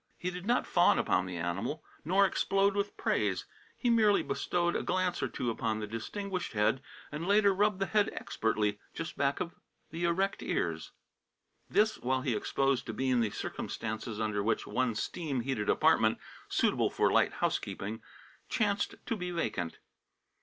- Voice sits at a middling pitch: Yes, medium, 150 Hz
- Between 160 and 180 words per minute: Yes, average, 165 wpm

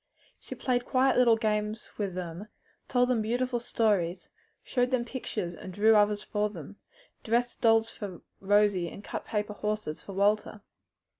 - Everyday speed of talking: Yes, average, 155 wpm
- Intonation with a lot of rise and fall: No, average, 2.7 semitones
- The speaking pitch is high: Yes, high, 210 Hz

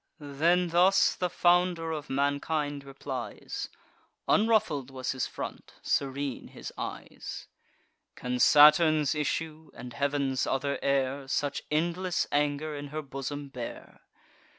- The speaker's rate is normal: No, slow, 115 wpm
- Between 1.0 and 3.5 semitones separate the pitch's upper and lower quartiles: Yes, average, 2.8 semitones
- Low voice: No, medium, 145 Hz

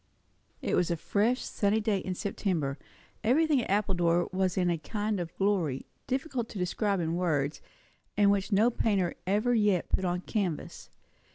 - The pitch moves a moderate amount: Yes, average, 3.4 semitones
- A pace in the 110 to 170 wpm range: Yes, average, 165 wpm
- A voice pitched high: Yes, high, 195 Hz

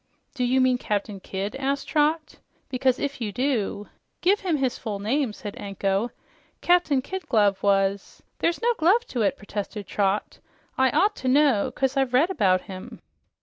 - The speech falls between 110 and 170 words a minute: No, average, 180 wpm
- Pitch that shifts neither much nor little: No, wide, 6.0 semitones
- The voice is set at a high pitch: Yes, very high, 255 Hz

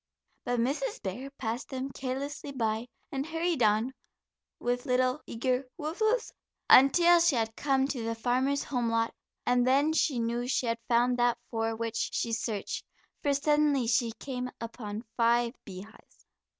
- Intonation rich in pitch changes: No, average, 3.2 semitones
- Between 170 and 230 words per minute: No, average, 155 wpm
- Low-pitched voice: No, very high, 250 Hz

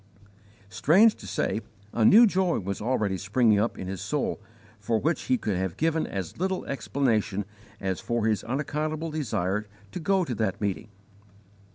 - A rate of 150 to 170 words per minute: Yes, average, 165 wpm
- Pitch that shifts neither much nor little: No, wide, 7.9 semitones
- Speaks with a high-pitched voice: No, low, 115 Hz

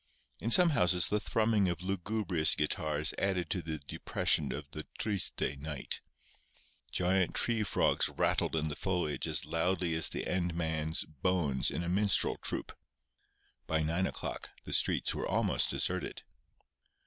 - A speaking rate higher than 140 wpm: Yes, average, 150 wpm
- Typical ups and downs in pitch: Yes, average, 3.6 semitones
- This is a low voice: Yes, very low, 85 Hz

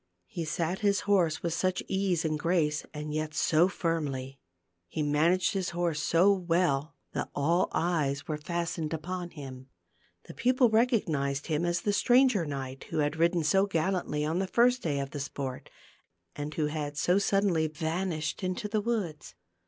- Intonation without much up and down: No, average, 3.7 semitones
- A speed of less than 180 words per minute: Yes, average, 170 wpm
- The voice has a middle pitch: Yes, medium, 165 Hz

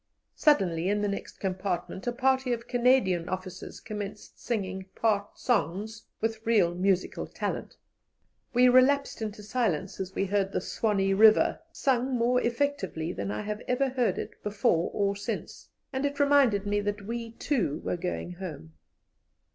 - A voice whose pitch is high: Yes, high, 210 Hz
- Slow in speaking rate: No, average, 155 wpm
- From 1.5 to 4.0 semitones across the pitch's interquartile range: No, average, 4.4 semitones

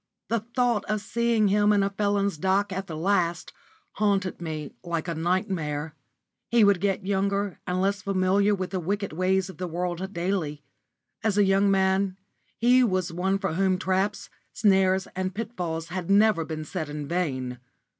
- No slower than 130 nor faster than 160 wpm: No, average, 170 wpm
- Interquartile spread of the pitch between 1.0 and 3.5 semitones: Yes, narrow, 2.6 semitones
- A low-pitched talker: No, high, 190 Hz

